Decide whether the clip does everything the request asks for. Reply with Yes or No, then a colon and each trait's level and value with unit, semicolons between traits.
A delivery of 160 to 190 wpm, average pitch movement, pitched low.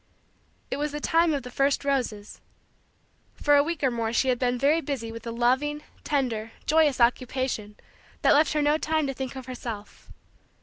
No: average, 185 wpm; average, 3.7 semitones; very high, 265 Hz